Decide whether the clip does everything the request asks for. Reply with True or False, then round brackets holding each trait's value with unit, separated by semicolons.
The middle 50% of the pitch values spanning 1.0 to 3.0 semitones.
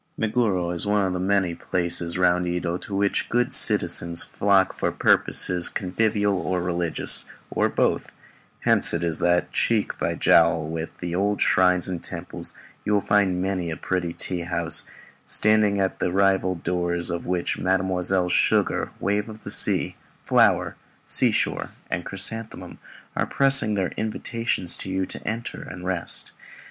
True (2.6 semitones)